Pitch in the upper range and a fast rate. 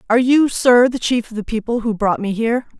Yes: high, 235 Hz; fast, 255 wpm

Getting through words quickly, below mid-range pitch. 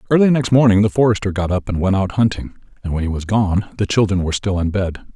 Yes: fast, 255 wpm; low, 100 Hz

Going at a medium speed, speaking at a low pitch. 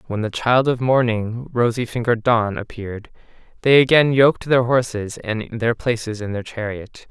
Yes: average, 170 wpm; low, 115 Hz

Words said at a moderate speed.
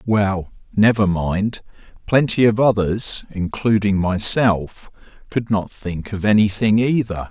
No: slow, 115 wpm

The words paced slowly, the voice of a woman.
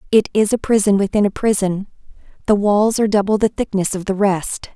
No: average, 200 wpm; female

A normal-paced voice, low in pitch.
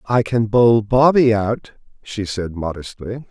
Yes: average, 145 wpm; low, 110 Hz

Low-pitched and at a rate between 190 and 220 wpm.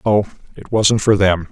Yes: low, 100 Hz; average, 200 wpm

